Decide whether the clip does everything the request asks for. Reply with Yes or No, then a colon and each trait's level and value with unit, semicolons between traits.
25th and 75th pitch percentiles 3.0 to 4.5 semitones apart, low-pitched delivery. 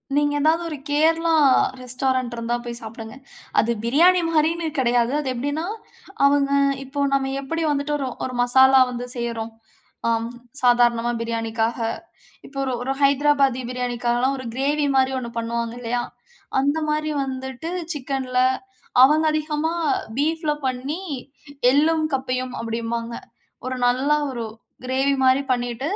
No: average, 3.3 semitones; very high, 260 Hz